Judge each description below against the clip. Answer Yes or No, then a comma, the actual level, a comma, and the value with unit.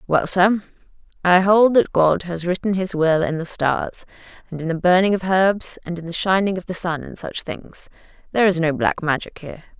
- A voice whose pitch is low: No, medium, 180 Hz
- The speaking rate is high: Yes, fast, 215 wpm